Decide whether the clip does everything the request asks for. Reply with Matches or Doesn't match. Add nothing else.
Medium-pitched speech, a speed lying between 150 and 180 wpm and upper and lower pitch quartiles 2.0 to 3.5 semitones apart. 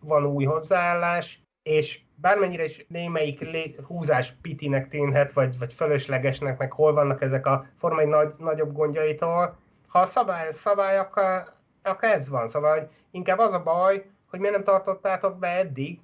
Doesn't match